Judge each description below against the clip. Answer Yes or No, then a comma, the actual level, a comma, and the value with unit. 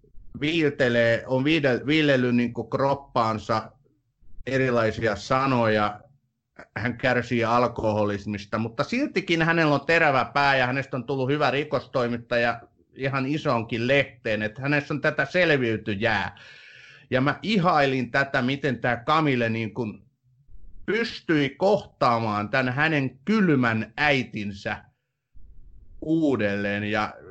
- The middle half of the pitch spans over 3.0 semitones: Yes, average, 4.0 semitones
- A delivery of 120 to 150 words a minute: No, average, 105 wpm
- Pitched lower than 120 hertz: No, low, 125 Hz